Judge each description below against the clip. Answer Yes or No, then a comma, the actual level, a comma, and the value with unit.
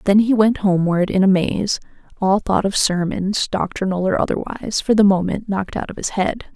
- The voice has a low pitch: No, high, 195 Hz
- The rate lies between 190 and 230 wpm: Yes, average, 200 wpm